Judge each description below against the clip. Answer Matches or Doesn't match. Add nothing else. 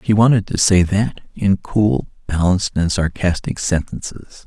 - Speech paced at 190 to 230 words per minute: Doesn't match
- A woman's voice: Doesn't match